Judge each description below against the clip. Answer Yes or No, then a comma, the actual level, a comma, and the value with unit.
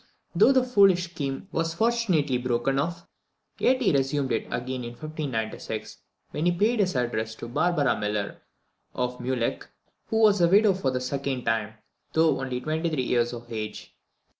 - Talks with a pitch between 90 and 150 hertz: Yes, medium, 140 Hz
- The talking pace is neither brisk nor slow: Yes, average, 165 wpm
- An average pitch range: No, wide, 6.1 semitones